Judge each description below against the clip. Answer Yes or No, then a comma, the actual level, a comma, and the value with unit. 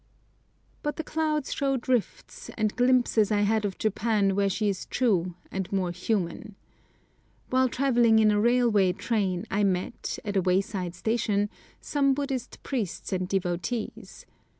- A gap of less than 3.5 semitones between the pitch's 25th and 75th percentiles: No, average, 4.2 semitones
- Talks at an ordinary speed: Yes, average, 145 wpm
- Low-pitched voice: No, high, 210 Hz